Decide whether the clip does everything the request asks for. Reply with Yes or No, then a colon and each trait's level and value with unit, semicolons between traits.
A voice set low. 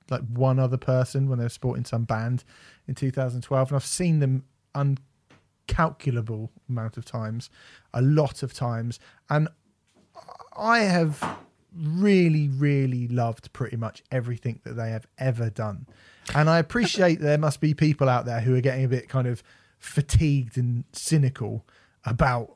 Yes: low, 130 Hz